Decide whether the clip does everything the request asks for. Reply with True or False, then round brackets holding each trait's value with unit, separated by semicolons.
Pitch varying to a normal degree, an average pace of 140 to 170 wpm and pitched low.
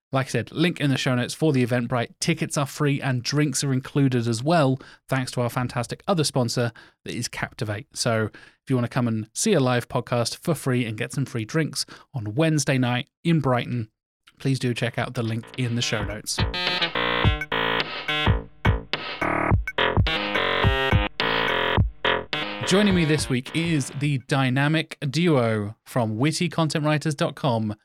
True (4.0 semitones; 155 wpm; 130 Hz)